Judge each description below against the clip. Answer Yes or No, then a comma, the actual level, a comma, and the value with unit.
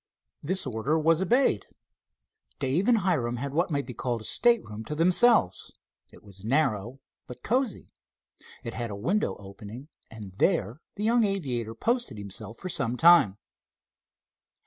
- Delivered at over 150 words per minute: No, average, 145 wpm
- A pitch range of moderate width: No, wide, 8.6 semitones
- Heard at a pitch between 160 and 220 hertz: No, low, 135 Hz